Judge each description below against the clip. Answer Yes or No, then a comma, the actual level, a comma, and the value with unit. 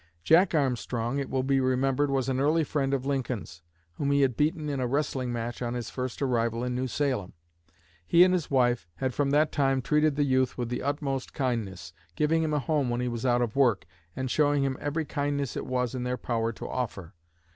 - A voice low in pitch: Yes, low, 130 Hz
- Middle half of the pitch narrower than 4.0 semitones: Yes, average, 2.8 semitones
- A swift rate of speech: Yes, fast, 220 wpm